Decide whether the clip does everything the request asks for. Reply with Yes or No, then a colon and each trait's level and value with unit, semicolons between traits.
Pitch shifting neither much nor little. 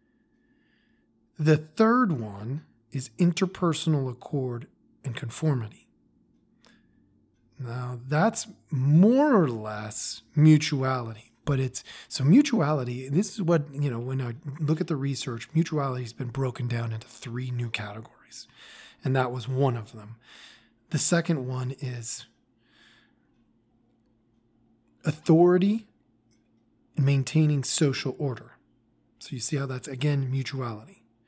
Yes: average, 4.6 semitones